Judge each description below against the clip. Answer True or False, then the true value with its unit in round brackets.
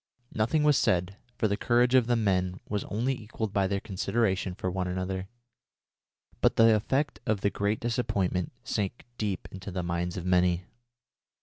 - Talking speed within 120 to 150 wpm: False (170 wpm)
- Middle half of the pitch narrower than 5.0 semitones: True (3.8 semitones)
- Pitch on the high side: False (100 Hz)